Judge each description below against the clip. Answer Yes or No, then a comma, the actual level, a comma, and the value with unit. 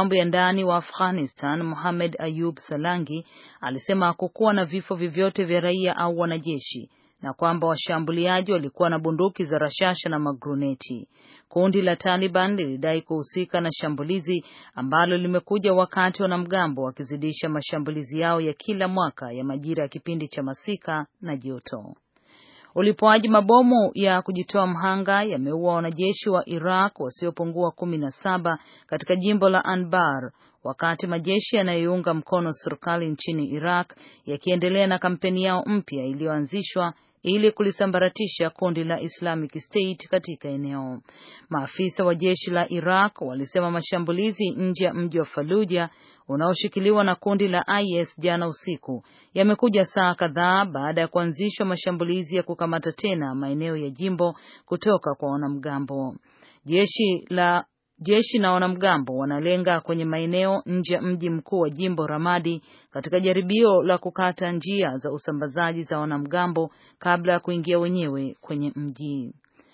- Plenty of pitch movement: No, average, 3.1 semitones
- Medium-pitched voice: Yes, medium, 175 Hz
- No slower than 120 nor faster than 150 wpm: Yes, average, 130 wpm